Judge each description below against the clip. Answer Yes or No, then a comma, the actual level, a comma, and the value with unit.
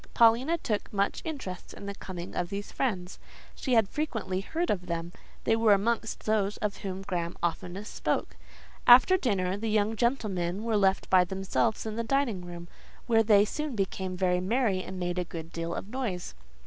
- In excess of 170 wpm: Yes, average, 185 wpm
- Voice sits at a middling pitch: No, high, 200 Hz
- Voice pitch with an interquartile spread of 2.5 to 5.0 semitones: Yes, average, 3.9 semitones